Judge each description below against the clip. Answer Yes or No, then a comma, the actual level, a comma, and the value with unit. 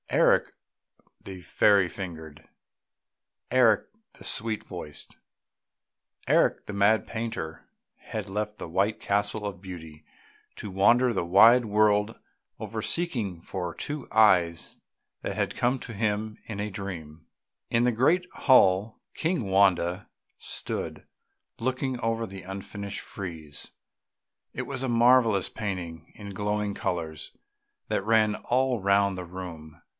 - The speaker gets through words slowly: Yes, slow, 125 wpm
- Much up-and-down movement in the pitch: No, average, 3.7 semitones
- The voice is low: Yes, low, 100 Hz